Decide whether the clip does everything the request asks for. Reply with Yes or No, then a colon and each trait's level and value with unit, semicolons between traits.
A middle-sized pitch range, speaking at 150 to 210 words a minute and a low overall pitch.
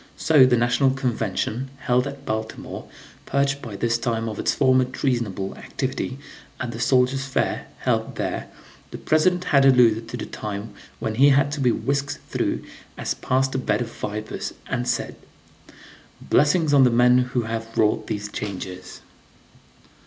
Yes: average, 3.3 semitones; average, 160 wpm; low, 125 Hz